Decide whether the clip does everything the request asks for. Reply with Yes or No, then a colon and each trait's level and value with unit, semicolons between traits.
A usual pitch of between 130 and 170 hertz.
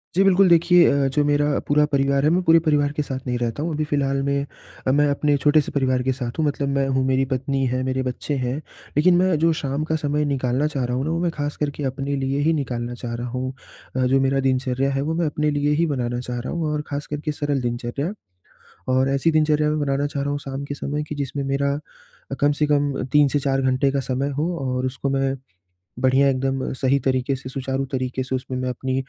Yes: medium, 140 Hz